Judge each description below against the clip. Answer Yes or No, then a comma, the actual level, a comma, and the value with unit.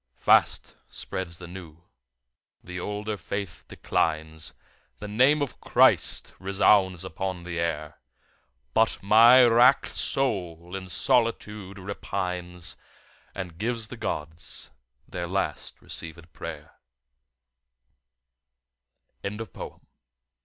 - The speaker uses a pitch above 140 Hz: No, very low, 95 Hz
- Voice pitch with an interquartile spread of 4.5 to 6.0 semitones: No, average, 3.9 semitones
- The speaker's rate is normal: No, slow, 100 wpm